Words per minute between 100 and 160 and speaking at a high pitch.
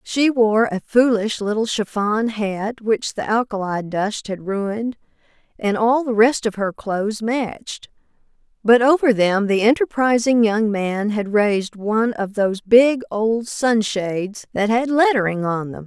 Yes: average, 155 wpm; high, 220 Hz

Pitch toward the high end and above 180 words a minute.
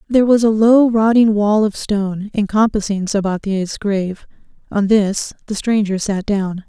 No: high, 205 Hz; average, 155 wpm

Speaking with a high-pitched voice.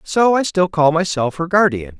No: medium, 170 Hz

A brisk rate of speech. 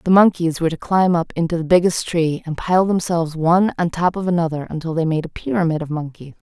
Yes: fast, 230 wpm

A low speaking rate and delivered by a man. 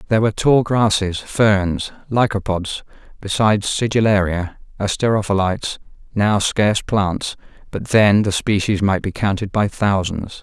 Yes: slow, 120 wpm; male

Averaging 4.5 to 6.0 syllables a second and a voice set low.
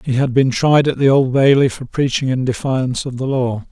Yes: 5.3 syllables/s; low, 130 Hz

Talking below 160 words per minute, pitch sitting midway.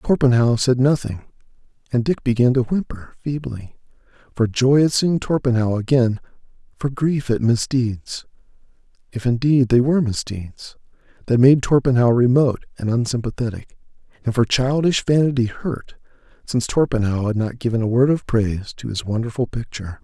No: average, 140 wpm; low, 125 Hz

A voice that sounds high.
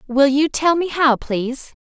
Yes: very high, 280 Hz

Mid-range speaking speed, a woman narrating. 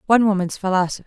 Yes: average, 170 wpm; female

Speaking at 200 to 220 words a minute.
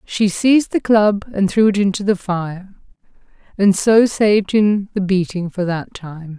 No: average, 180 wpm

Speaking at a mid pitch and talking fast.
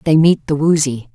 Yes: medium, 150 Hz; fast, 210 wpm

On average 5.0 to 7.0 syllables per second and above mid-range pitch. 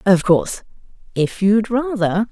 No: 4.2 syllables/s; high, 205 Hz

